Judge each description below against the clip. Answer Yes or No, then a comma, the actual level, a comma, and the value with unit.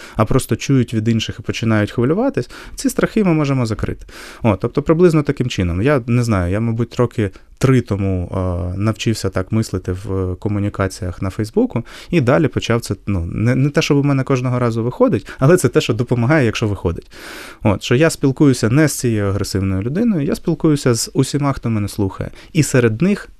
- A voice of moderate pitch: No, low, 120 Hz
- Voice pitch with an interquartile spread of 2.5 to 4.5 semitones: No, wide, 5.6 semitones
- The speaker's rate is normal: No, fast, 185 wpm